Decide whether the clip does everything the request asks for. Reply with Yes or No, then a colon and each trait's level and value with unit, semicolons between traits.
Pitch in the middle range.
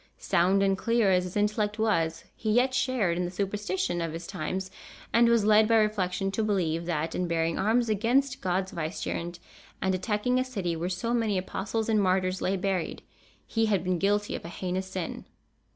No: high, 195 Hz